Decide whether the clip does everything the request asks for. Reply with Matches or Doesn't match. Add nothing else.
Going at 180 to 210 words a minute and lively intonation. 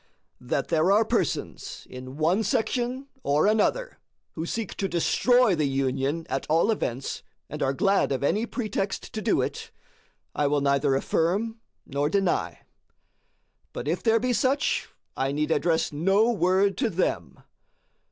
Doesn't match